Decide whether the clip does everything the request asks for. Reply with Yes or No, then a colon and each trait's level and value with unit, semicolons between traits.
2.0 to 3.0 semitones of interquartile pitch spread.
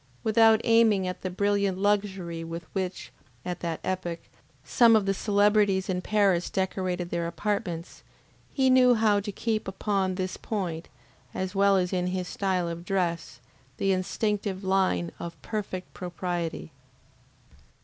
Yes: narrow, 2.4 semitones